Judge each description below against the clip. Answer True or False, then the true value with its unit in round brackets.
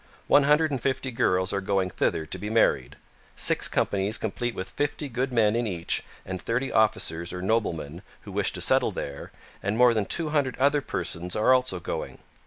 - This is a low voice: True (110 Hz)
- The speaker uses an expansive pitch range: True (5.8 semitones)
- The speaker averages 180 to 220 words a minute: True (190 wpm)